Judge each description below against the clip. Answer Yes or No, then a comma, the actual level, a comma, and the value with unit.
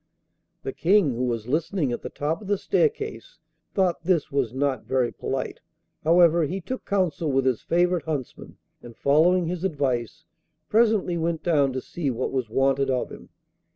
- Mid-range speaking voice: Yes, medium, 160 Hz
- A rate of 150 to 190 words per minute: Yes, average, 170 wpm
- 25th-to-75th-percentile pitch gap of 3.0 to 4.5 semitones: No, average, 5.3 semitones